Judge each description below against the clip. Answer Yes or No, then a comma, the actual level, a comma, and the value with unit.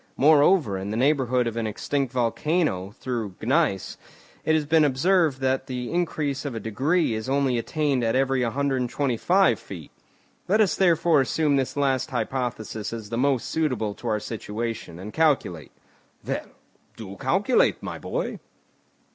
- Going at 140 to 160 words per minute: Yes, average, 150 wpm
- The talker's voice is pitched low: Yes, low, 130 Hz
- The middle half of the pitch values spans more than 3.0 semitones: Yes, average, 4.8 semitones